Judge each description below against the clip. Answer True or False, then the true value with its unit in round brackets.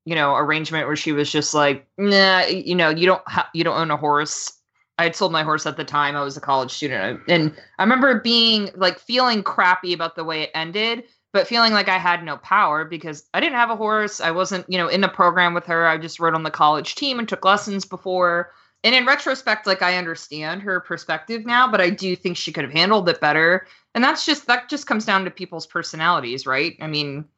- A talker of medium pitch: True (175 Hz)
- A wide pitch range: False (4.6 semitones)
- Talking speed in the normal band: False (240 wpm)